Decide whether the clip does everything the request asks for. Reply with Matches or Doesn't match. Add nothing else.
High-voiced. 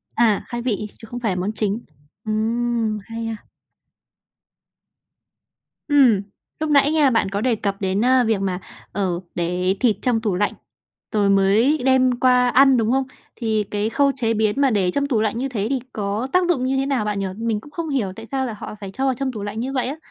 Matches